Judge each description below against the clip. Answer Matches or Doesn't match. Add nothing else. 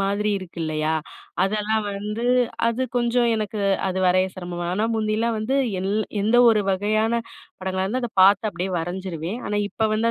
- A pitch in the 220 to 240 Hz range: Doesn't match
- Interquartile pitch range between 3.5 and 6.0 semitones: Doesn't match